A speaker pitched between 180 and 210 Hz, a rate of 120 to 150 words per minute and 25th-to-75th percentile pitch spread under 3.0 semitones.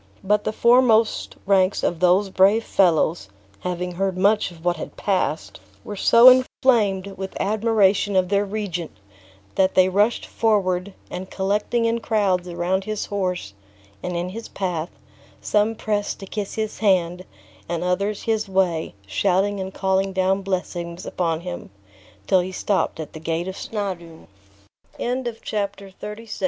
Yes: high, 190 Hz; average, 145 wpm; narrow, 2.5 semitones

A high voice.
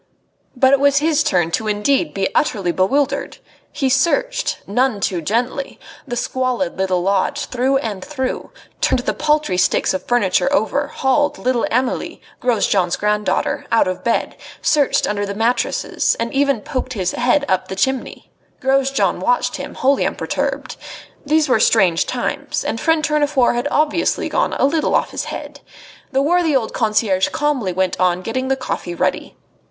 Yes: very high, 255 Hz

